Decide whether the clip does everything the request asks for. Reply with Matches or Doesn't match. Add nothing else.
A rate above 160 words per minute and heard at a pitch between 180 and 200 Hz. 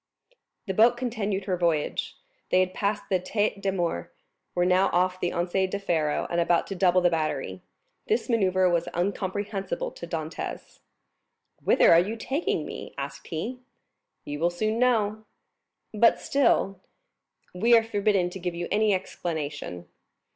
Doesn't match